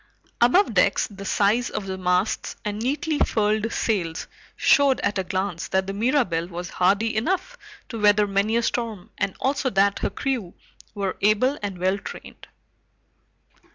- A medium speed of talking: Yes, average, 155 wpm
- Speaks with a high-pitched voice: Yes, high, 205 Hz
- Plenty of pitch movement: No, average, 3.9 semitones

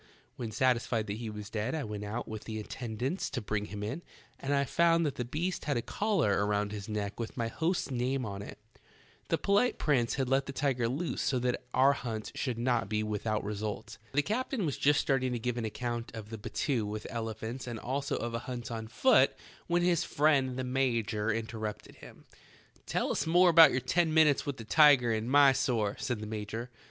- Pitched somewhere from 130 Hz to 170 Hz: No, low, 120 Hz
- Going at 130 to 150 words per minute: No, fast, 205 wpm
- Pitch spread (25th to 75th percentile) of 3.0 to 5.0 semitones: Yes, average, 4.3 semitones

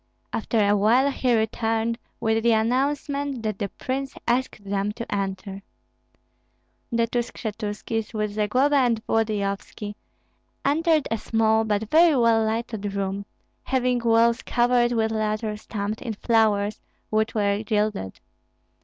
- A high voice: Yes, high, 225 Hz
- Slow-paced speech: Yes, slow, 130 wpm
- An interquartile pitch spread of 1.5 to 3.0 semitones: Yes, narrow, 2.4 semitones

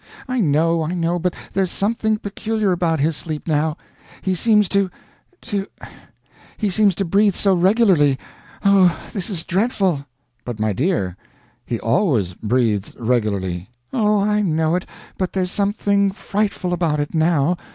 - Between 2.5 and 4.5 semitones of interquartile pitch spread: No, average, 5.2 semitones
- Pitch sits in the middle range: Yes, medium, 180 Hz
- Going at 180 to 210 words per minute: No, average, 150 wpm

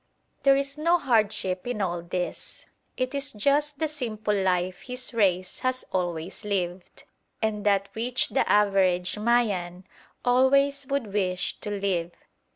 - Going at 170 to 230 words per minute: No, average, 140 wpm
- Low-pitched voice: No, high, 210 Hz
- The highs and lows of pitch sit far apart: Yes, wide, 5.8 semitones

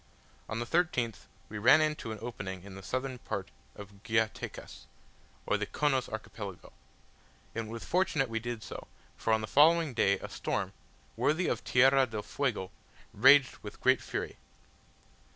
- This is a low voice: Yes, low, 115 Hz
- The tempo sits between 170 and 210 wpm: No, average, 160 wpm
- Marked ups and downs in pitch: No, average, 4.2 semitones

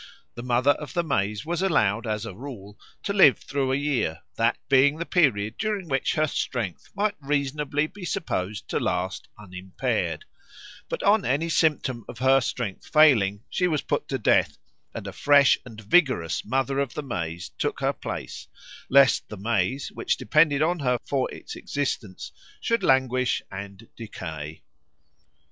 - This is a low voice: Yes, low, 130 Hz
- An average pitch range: No, wide, 6.1 semitones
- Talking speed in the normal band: Yes, average, 160 wpm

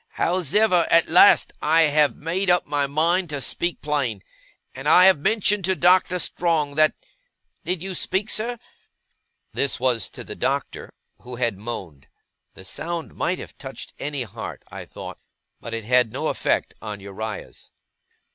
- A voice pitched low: No, medium, 155 Hz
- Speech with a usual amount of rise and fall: No, wide, 6.3 semitones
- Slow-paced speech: No, average, 155 wpm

